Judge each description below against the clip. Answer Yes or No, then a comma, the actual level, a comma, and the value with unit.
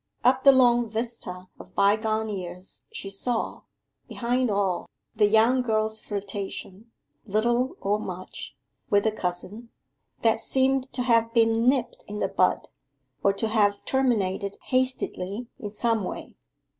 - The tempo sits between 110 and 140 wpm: Yes, slow, 135 wpm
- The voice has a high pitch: Yes, high, 220 Hz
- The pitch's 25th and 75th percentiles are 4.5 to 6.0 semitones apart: No, average, 3.2 semitones